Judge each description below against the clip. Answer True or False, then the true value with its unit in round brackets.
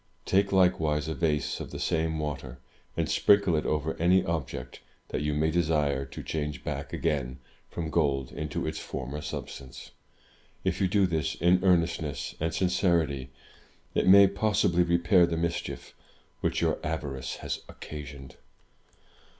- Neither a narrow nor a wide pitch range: True (3.3 semitones)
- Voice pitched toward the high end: False (80 Hz)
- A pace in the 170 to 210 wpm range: False (145 wpm)